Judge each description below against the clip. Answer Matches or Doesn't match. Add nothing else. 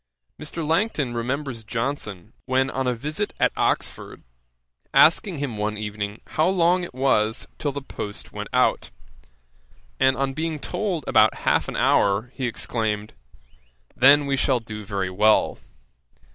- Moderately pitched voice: Doesn't match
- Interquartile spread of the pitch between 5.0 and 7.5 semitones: Matches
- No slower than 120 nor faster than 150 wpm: Matches